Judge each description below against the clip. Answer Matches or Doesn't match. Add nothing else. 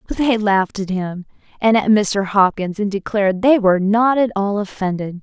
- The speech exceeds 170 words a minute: Matches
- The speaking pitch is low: Doesn't match